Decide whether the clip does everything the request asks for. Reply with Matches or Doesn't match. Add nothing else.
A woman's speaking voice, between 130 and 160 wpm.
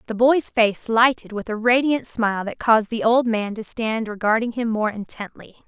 Doesn't match